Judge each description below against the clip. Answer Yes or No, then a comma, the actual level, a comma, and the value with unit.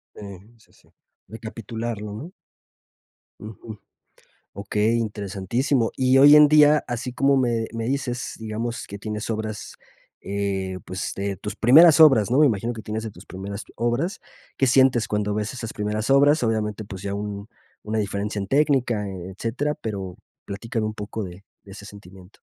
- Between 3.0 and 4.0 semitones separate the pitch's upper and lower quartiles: Yes, average, 3.3 semitones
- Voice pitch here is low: Yes, low, 110 Hz